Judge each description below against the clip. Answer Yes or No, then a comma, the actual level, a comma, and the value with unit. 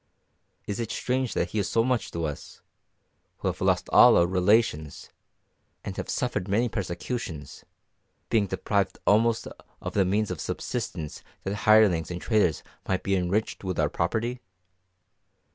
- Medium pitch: No, low, 100 Hz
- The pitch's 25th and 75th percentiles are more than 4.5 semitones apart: No, average, 4.0 semitones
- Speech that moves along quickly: No, average, 150 wpm